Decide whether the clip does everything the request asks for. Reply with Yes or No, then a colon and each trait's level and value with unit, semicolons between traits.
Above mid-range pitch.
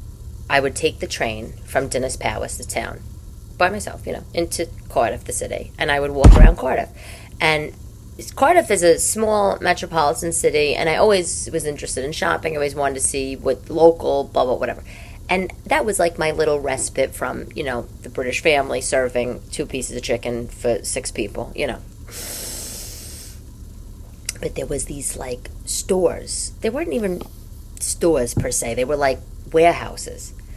No: medium, 140 Hz